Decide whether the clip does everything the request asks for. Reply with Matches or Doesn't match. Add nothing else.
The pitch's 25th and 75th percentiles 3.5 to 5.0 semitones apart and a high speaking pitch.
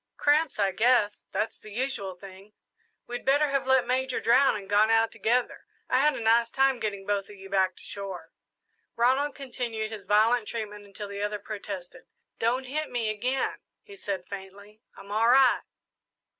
Matches